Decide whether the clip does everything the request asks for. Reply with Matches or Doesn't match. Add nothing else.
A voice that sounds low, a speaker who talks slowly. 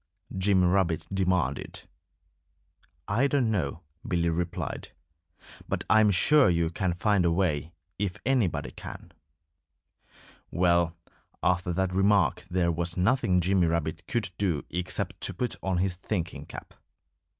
Matches